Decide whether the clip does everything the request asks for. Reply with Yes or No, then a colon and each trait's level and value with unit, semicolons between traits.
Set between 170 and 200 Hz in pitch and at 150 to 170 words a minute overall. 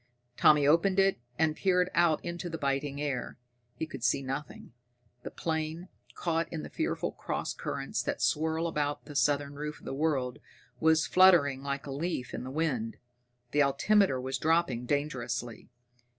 No: medium, 150 Hz; average, 165 wpm